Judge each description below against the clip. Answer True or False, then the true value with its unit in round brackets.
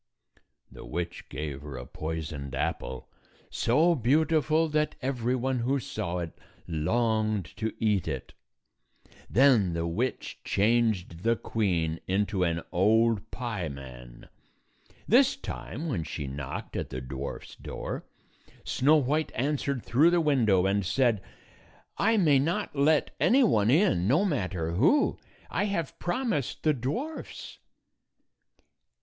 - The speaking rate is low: True (130 wpm)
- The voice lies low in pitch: True (115 Hz)